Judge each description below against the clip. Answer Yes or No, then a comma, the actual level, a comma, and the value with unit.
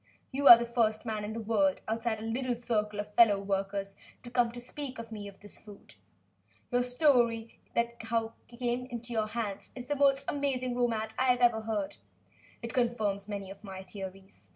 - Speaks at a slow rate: No, average, 200 wpm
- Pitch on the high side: Yes, high, 230 Hz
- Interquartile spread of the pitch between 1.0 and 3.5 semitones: Yes, average, 2.9 semitones